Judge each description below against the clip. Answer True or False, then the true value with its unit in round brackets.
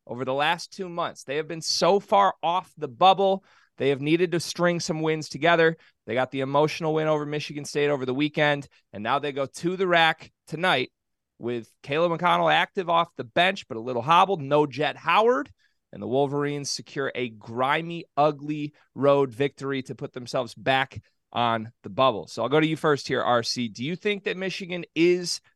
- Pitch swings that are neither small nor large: True (4.3 semitones)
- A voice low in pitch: False (150 Hz)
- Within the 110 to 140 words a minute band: False (195 wpm)